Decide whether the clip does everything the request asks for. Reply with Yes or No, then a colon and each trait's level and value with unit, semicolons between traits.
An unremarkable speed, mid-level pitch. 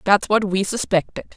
No: average, 175 wpm; high, 200 Hz